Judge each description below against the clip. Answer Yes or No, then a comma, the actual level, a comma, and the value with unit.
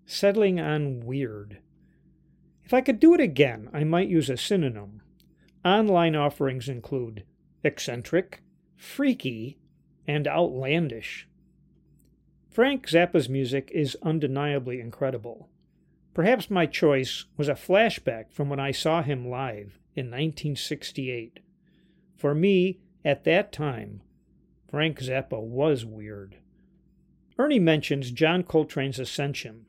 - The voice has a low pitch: No, medium, 150 Hz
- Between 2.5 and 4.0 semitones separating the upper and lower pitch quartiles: No, average, 5.1 semitones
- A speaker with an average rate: No, slow, 110 wpm